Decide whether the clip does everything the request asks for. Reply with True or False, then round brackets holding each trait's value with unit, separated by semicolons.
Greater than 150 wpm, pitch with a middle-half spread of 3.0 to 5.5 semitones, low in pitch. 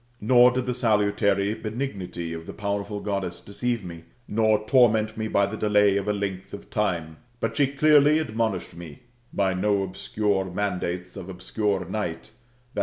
False (165 wpm; 2.6 semitones; 100 Hz)